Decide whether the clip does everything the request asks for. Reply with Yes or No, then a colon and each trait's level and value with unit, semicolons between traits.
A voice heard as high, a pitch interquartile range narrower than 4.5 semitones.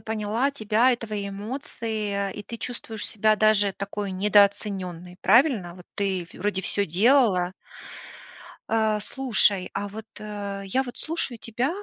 Yes: high, 210 Hz; narrow, 2.4 semitones